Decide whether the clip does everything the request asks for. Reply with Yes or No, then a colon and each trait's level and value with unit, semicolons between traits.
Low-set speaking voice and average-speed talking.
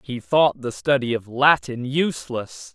Yes: low, 130 Hz; average, 155 wpm